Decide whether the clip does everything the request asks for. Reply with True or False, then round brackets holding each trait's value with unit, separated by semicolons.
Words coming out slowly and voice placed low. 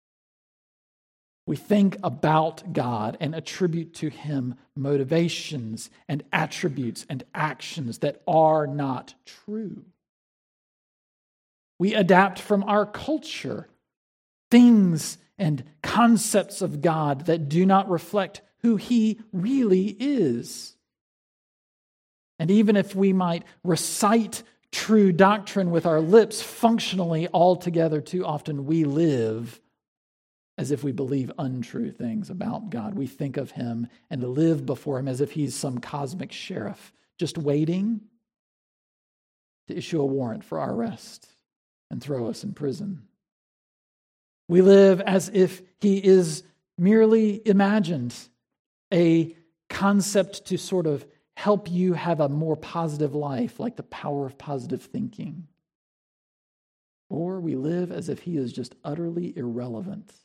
False (125 wpm; 170 Hz)